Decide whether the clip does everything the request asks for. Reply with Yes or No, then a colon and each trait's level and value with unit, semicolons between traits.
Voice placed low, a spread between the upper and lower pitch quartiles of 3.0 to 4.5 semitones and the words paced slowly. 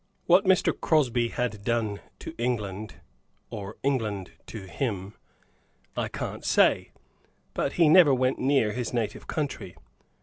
No: low, 120 Hz; average, 4.9 semitones; slow, 130 wpm